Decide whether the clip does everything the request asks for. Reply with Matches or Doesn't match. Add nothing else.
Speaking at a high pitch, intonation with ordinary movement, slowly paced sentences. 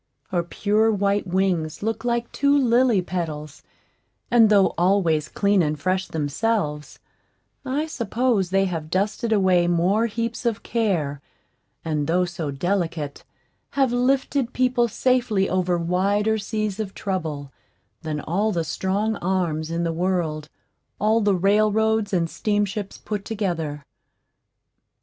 Matches